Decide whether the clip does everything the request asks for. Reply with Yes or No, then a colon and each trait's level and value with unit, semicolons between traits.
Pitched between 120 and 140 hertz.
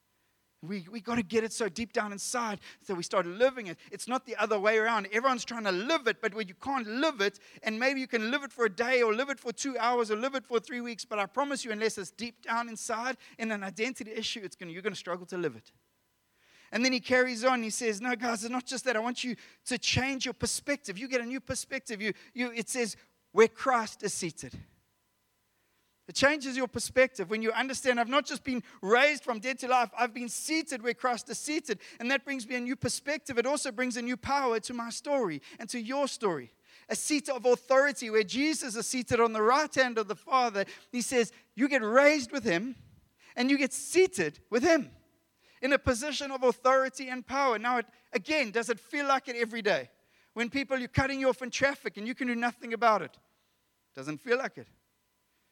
No: high, 240 Hz